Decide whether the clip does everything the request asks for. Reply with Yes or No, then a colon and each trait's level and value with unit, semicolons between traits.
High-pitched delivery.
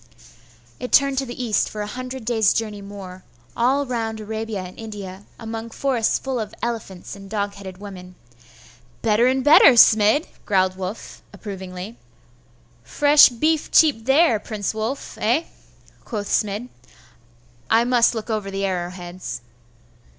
Yes: high, 220 Hz